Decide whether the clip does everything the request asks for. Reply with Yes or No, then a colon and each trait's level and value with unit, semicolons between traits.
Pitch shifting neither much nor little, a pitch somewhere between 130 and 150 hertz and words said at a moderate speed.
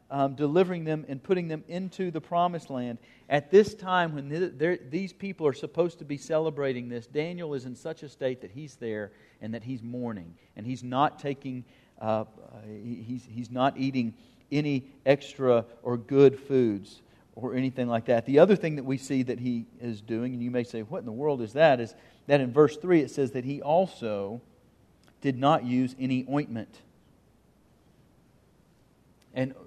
Yes: average, 3.9 semitones; low, 135 Hz; average, 180 wpm